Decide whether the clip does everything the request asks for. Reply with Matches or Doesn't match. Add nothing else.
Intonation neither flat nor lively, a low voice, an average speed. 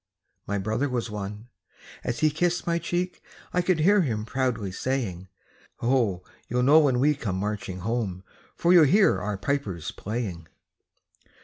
Doesn't match